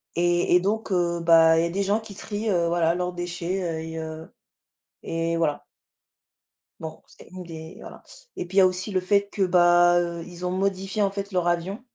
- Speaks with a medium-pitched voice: Yes, medium, 175 Hz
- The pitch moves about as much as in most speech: No, narrow, 2.3 semitones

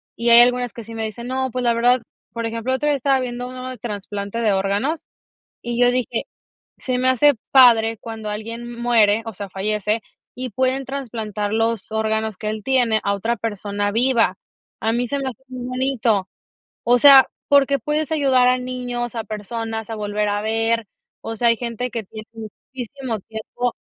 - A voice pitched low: No, high, 235 Hz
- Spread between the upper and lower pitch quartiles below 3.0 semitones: Yes, narrow, 2.6 semitones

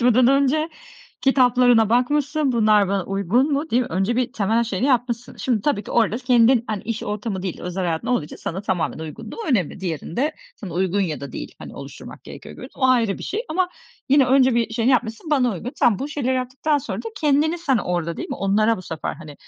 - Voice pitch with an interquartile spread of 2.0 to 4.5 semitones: No, average, 5.0 semitones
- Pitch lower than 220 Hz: No, high, 235 Hz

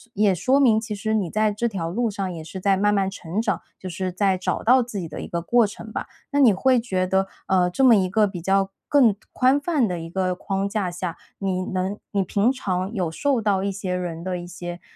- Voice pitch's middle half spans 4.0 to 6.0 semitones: No, average, 3.2 semitones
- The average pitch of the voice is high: Yes, high, 195 Hz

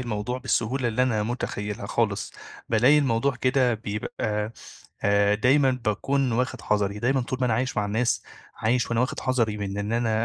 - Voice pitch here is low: Yes, low, 115 Hz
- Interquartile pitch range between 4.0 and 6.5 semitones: No, average, 3.3 semitones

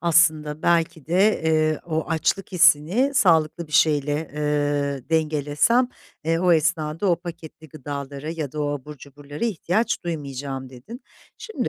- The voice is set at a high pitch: No, medium, 155 Hz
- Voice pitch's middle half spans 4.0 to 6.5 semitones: No, average, 2.7 semitones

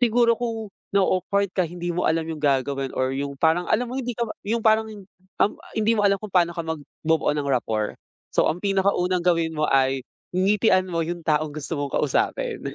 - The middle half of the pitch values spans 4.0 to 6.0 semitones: Yes, average, 5.0 semitones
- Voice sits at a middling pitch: Yes, medium, 175 Hz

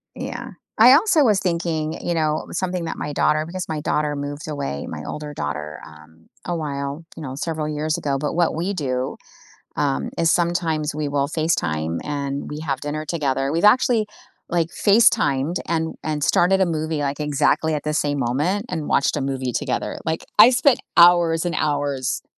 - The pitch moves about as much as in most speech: Yes, average, 3.3 semitones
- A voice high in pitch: No, medium, 155 Hz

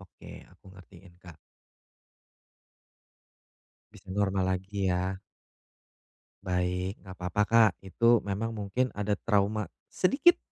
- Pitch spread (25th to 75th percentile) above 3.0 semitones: No, narrow, 2.5 semitones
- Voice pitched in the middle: No, low, 100 Hz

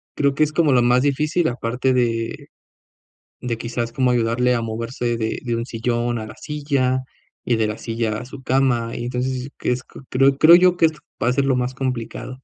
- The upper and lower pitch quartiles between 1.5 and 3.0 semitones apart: Yes, narrow, 2.4 semitones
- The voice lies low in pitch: Yes, low, 125 Hz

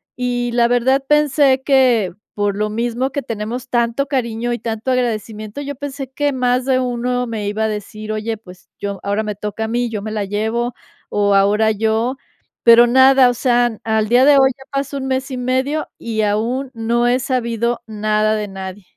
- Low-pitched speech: No, high, 235 Hz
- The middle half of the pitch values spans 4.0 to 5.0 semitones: No, average, 3.2 semitones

